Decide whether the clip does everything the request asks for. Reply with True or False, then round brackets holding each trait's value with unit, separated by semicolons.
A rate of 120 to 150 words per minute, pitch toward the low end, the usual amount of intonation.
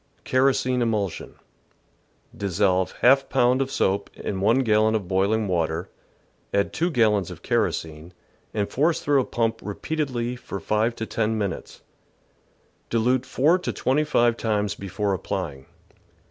True (140 wpm; 110 Hz; 4.4 semitones)